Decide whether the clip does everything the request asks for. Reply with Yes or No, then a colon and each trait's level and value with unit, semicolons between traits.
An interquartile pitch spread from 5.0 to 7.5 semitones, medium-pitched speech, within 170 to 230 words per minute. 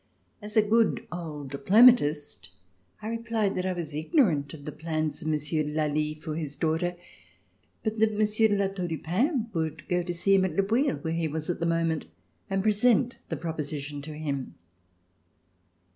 Yes: wide, 5.4 semitones; medium, 165 Hz; average, 185 wpm